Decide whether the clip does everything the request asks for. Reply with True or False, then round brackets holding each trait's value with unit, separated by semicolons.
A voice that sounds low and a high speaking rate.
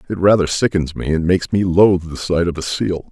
True (90 Hz; 250 wpm)